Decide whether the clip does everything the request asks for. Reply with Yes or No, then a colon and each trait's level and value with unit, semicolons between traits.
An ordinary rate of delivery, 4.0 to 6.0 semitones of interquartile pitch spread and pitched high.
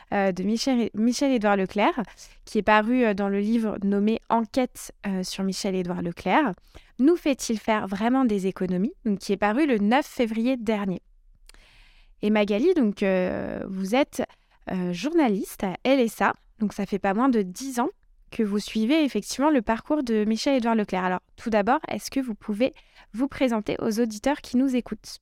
Yes: average, 165 wpm; average, 4.3 semitones; high, 220 Hz